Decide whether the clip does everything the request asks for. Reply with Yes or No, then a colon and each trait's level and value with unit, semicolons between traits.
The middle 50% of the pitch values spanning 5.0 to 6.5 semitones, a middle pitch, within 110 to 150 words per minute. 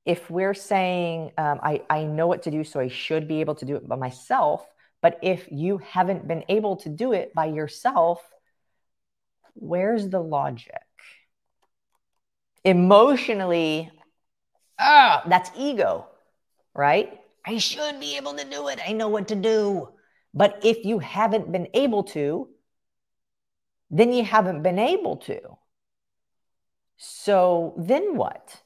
Yes: wide, 5.6 semitones; medium, 180 Hz; average, 140 wpm